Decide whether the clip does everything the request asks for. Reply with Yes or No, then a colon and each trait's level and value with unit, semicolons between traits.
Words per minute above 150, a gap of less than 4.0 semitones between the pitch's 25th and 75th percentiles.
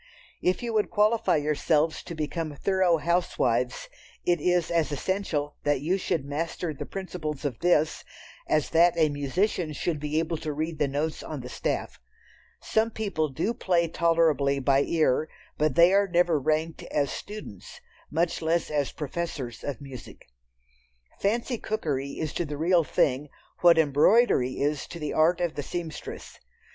Yes: average, 160 wpm; average, 3.2 semitones